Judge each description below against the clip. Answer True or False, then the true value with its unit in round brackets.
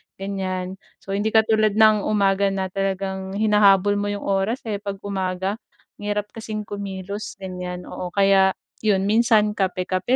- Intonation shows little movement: True (1.6 semitones)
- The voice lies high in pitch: True (200 Hz)